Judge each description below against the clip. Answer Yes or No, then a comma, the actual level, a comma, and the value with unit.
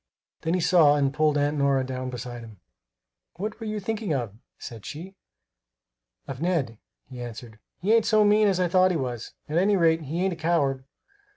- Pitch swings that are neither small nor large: No, wide, 6.1 semitones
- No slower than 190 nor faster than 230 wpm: Yes, average, 195 wpm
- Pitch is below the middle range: No, medium, 155 Hz